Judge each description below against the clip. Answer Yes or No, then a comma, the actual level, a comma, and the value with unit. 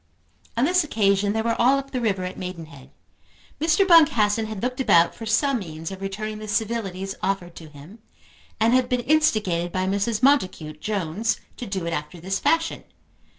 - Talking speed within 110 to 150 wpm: No, average, 180 wpm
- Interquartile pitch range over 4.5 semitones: Yes, average, 4.9 semitones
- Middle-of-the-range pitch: No, high, 210 Hz